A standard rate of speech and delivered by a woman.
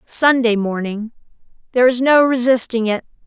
No: slow, 110 wpm; female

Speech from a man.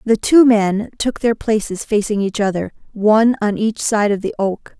No: female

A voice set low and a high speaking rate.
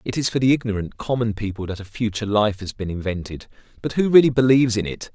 Yes: low, 110 Hz; fast, 235 wpm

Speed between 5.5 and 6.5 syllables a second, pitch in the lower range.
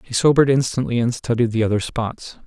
Yes: 6.0 syllables/s; low, 120 Hz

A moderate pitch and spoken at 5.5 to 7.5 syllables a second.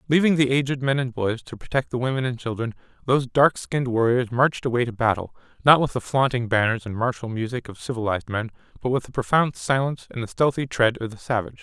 No: low, 125 Hz; 6.4 syllables/s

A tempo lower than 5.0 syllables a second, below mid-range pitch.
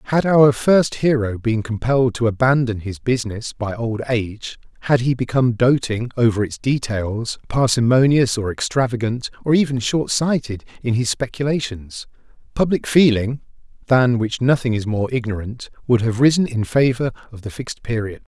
No: 5.1 syllables/s; low, 120 Hz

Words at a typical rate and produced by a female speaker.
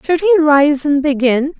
Yes: average, 190 wpm; female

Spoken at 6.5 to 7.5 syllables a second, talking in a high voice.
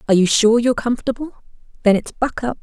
Yes: 7.4 syllables/s; high, 230 Hz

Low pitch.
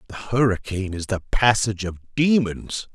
Yes: low, 105 Hz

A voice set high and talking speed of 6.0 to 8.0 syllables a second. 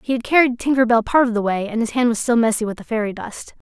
Yes: high, 235 Hz; 6.6 syllables/s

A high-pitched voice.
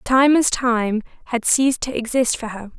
Yes: high, 245 Hz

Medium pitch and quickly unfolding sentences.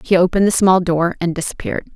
Yes: medium, 180 Hz; fast, 215 wpm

